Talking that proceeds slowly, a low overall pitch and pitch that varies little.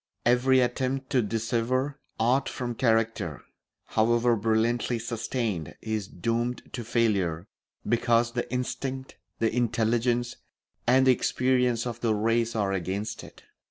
Yes: slow, 125 wpm; low, 120 Hz; narrow, 1.9 semitones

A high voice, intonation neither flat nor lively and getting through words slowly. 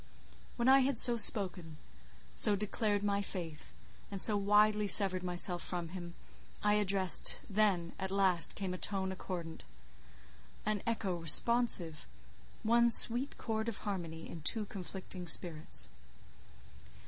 Yes: high, 195 Hz; average, 3.3 semitones; slow, 125 wpm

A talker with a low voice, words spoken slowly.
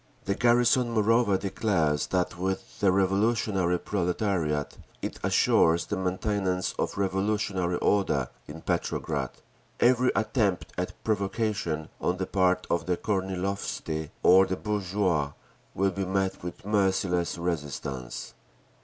Yes: very low, 95 Hz; slow, 120 wpm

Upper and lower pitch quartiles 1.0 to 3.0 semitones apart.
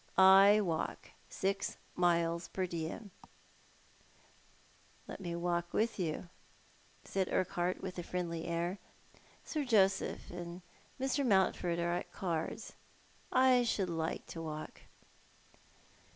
Yes: narrow, 2.5 semitones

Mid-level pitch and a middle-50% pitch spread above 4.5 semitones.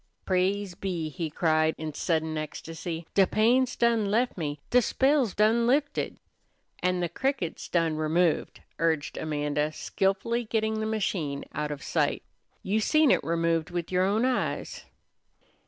Yes: medium, 180 Hz; wide, 5.5 semitones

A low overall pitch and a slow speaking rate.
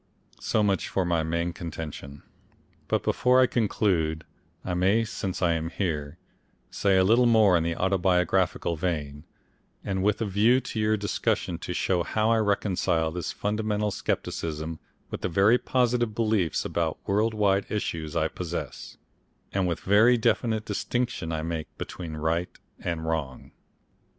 No: very low, 95 Hz; average, 150 wpm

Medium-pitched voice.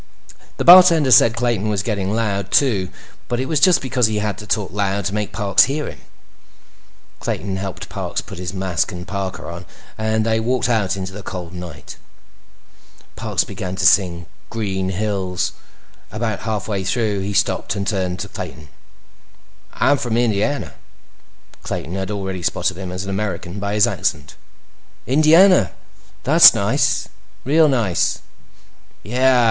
No: low, 100 Hz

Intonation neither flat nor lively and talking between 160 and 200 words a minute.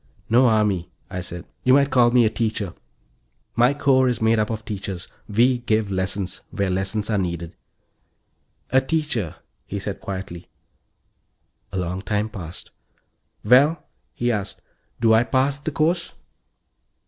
No: average, 4.7 semitones; average, 145 wpm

